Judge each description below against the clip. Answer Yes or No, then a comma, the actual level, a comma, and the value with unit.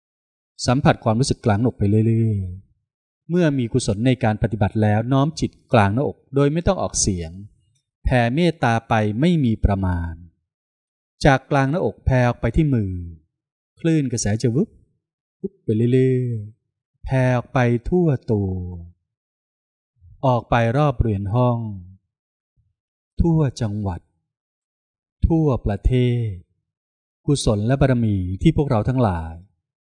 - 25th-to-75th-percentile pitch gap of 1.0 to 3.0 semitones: No, average, 4.5 semitones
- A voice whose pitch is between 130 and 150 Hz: No, low, 115 Hz